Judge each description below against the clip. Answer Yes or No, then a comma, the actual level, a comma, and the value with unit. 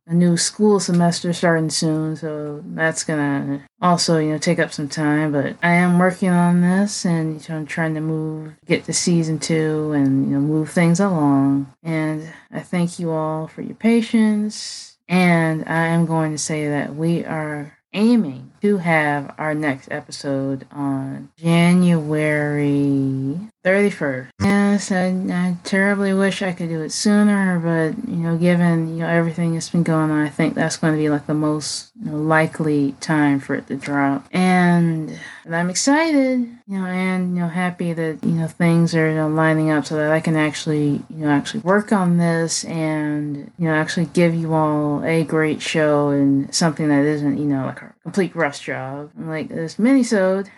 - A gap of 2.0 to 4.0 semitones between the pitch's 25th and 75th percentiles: Yes, average, 2.9 semitones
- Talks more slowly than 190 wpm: Yes, average, 180 wpm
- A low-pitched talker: No, medium, 160 Hz